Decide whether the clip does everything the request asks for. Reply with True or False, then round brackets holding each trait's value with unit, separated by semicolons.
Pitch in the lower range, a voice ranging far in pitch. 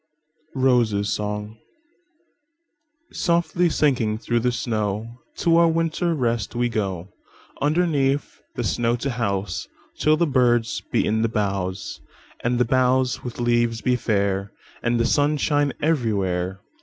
True (120 Hz; 5.9 semitones)